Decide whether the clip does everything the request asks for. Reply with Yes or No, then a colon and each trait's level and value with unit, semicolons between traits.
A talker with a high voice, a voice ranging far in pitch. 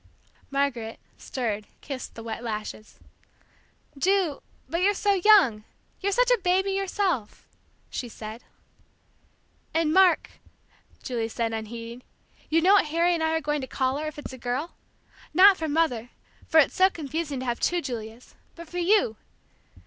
Yes: very high, 300 Hz; wide, 7.1 semitones